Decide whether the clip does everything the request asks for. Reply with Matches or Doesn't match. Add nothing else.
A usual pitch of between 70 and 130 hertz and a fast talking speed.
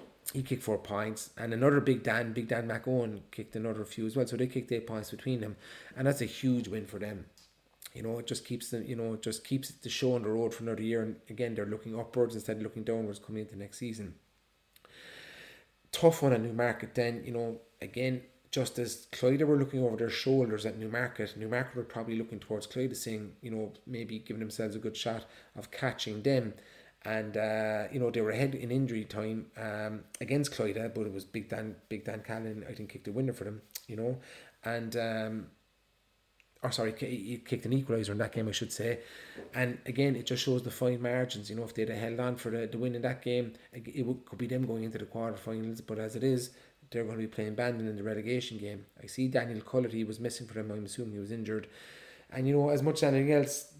Matches